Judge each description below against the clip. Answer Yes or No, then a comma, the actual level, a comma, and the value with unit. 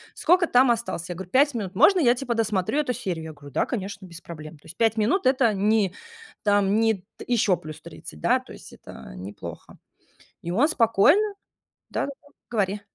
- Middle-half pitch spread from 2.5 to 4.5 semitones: No, wide, 5.5 semitones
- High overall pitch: Yes, high, 205 Hz